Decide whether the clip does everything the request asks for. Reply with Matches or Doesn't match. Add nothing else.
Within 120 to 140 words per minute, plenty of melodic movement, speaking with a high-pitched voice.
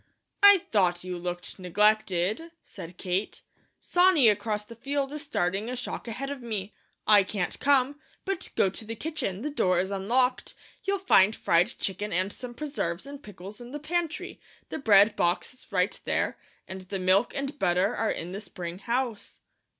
Doesn't match